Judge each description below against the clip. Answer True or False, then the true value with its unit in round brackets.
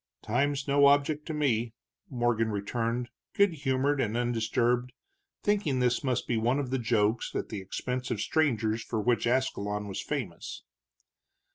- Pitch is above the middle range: False (125 Hz)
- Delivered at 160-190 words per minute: False (150 wpm)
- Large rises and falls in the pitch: False (3.7 semitones)